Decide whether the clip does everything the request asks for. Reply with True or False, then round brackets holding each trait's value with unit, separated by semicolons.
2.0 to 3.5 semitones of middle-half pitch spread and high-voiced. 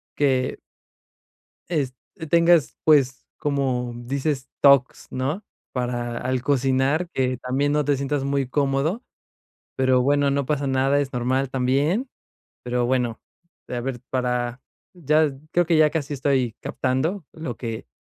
False (2.5 semitones; 135 Hz)